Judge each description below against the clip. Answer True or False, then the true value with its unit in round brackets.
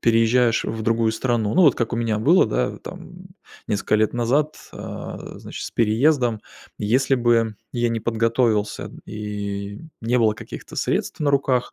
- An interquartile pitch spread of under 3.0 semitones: True (2.4 semitones)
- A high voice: False (115 Hz)